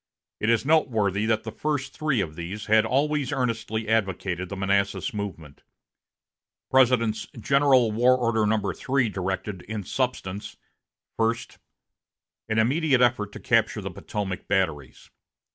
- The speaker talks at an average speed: No, slow, 130 wpm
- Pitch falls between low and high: No, low, 110 Hz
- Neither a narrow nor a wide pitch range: Yes, average, 4.3 semitones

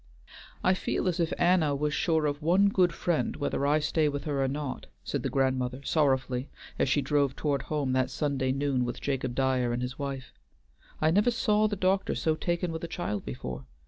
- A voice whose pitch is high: No, medium, 145 Hz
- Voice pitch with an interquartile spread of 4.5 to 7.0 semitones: No, average, 4.0 semitones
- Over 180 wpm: Yes, fast, 205 wpm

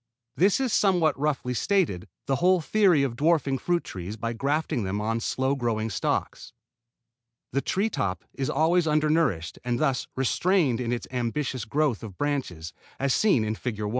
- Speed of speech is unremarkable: Yes, average, 170 wpm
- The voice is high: No, low, 135 Hz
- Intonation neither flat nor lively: No, wide, 5.9 semitones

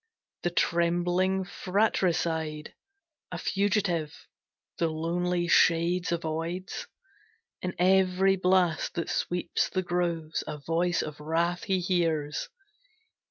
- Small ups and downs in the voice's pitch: Yes, narrow, 1.9 semitones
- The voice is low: No, medium, 175 Hz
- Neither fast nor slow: No, slow, 100 wpm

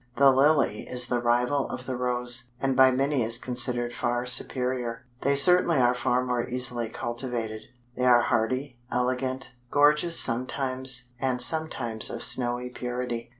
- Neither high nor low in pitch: No, low, 125 Hz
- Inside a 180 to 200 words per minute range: No, average, 150 wpm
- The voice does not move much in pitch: Yes, narrow, 1.5 semitones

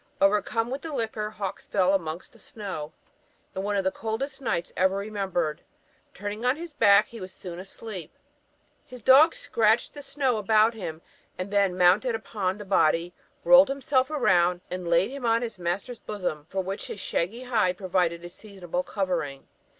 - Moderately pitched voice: No, high, 200 Hz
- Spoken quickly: No, average, 175 wpm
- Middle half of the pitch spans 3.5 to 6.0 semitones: Yes, average, 4.2 semitones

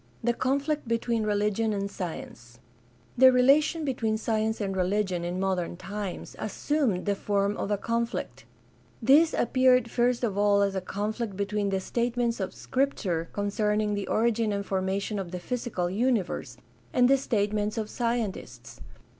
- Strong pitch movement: No, average, 3.4 semitones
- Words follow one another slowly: No, average, 155 wpm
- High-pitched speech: Yes, high, 210 Hz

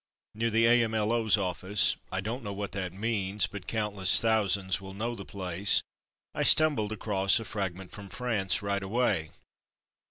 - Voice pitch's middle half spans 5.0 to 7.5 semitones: No, average, 2.7 semitones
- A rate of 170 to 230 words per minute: No, average, 155 wpm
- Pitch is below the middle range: Yes, low, 100 Hz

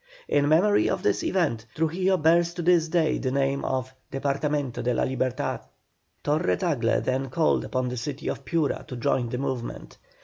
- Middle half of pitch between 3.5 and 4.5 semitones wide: Yes, average, 4.1 semitones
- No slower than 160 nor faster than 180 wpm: Yes, average, 175 wpm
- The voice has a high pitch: No, medium, 140 Hz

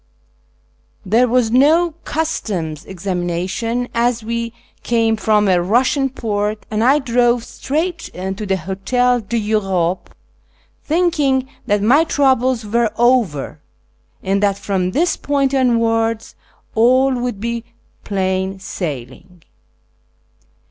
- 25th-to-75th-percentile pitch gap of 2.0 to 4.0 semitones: No, average, 4.6 semitones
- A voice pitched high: Yes, high, 230 Hz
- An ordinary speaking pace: No, slow, 110 wpm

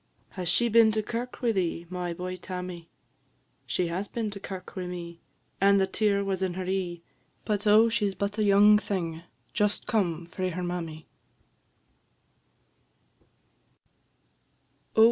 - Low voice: No, high, 190 Hz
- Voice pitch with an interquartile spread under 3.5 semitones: Yes, average, 2.9 semitones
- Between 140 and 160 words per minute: Yes, average, 145 wpm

